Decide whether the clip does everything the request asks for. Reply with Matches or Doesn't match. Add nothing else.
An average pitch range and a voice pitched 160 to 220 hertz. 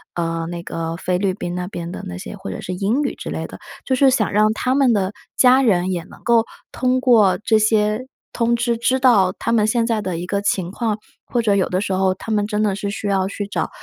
Matches